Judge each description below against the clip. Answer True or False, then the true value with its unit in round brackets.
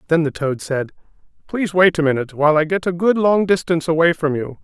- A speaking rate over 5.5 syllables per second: True (6.5 syllables/s)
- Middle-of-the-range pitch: True (165 Hz)